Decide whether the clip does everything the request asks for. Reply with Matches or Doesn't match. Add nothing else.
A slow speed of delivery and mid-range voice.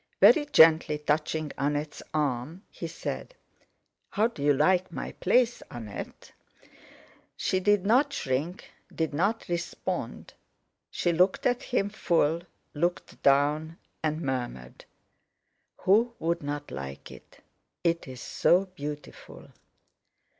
Matches